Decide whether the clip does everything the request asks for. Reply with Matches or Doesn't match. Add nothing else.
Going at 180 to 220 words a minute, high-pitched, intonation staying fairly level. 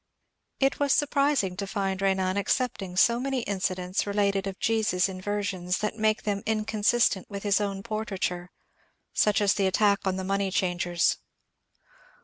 Doesn't match